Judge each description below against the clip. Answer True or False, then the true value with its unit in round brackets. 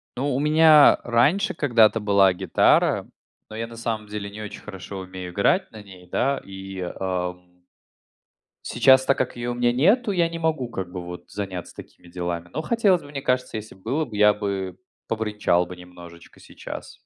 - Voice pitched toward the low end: True (105 Hz)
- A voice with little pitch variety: False (6.1 semitones)